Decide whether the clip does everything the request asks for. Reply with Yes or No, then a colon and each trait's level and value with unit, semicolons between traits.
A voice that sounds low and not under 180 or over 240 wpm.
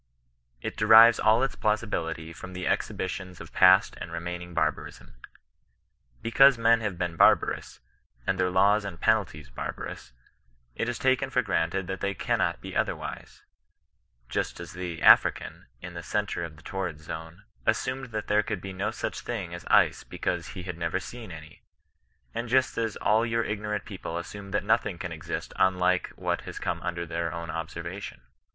No: very low, 95 Hz; average, 170 wpm